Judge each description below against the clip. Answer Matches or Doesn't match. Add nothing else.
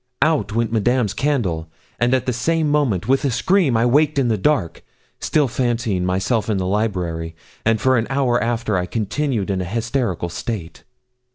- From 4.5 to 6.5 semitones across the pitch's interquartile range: Matches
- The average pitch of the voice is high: Doesn't match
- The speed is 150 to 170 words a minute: Doesn't match